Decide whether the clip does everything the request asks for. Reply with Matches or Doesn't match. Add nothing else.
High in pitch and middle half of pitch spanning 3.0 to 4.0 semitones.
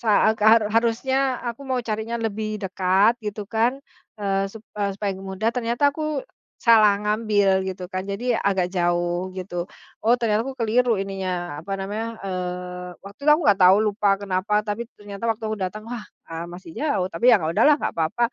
Matches